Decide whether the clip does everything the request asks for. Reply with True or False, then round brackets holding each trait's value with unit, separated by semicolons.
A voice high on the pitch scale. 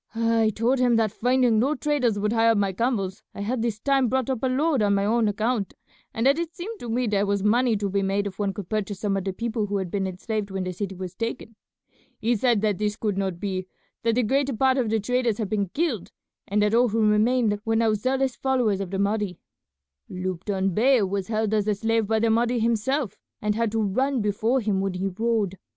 True (220 Hz)